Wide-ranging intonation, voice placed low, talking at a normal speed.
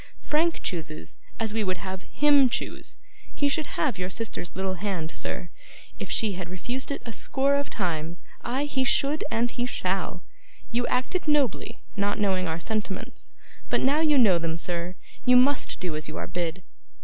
No: wide, 6.9 semitones; high, 210 Hz; average, 180 wpm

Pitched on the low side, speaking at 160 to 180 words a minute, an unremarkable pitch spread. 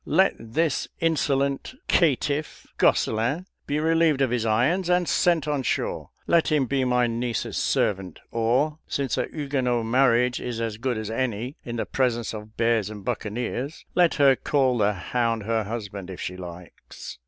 Yes: low, 125 Hz; average, 165 wpm; average, 4.2 semitones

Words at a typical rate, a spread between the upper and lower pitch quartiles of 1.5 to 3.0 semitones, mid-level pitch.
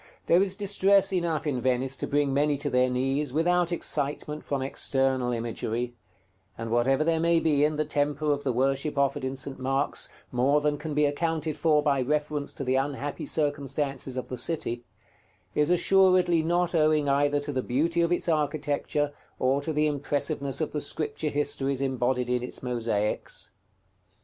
Yes: average, 175 wpm; narrow, 2.6 semitones; medium, 145 Hz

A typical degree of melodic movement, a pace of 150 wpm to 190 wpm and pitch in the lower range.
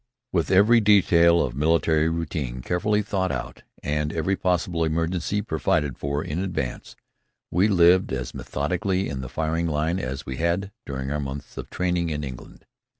Yes: average, 4.0 semitones; average, 160 wpm; very low, 80 Hz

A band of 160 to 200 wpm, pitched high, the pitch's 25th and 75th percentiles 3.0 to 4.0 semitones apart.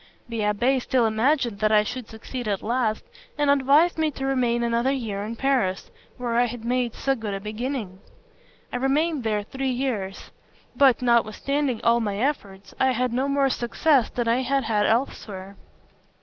Yes: average, 175 wpm; high, 240 Hz; average, 3.7 semitones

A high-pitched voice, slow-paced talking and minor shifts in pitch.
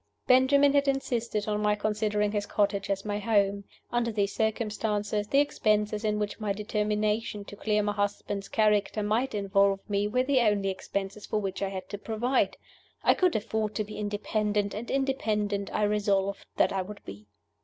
No: high, 210 Hz; average, 175 wpm; narrow, 1.3 semitones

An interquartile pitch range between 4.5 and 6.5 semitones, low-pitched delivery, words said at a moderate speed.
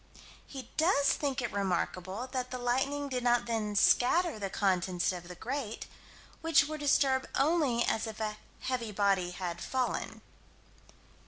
No: wide, 5.4 semitones; high, 240 Hz; average, 150 wpm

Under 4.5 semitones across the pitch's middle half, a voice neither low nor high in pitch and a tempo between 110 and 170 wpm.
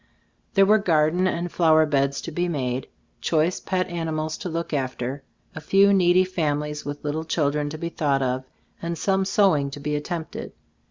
No: average, 3.3 semitones; medium, 160 Hz; average, 180 wpm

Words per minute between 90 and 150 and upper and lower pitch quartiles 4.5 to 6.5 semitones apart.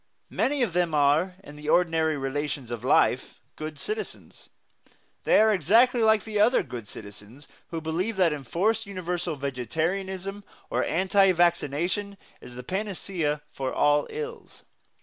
Yes: average, 140 wpm; wide, 5.4 semitones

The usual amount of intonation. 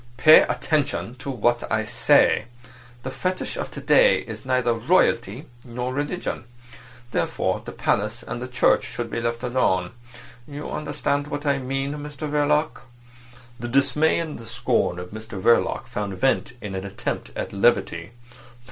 Yes: average, 4.2 semitones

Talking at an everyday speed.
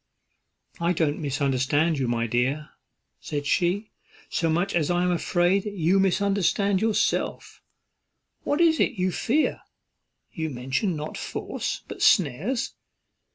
No: slow, 125 wpm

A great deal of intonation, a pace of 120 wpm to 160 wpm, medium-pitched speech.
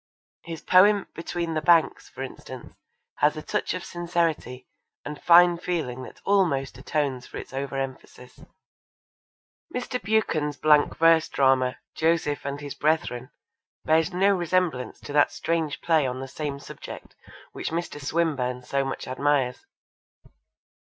No: average, 4.0 semitones; average, 140 wpm; medium, 150 Hz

